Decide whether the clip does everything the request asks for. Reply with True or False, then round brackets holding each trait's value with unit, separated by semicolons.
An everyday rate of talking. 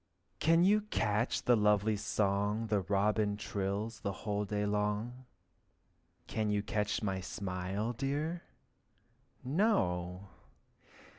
False (100 wpm)